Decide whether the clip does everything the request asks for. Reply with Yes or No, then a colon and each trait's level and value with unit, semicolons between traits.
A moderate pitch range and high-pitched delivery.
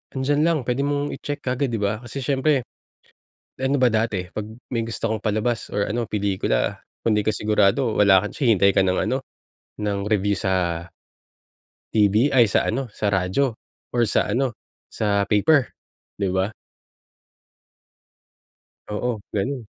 No: average, 4.2 semitones; low, 110 Hz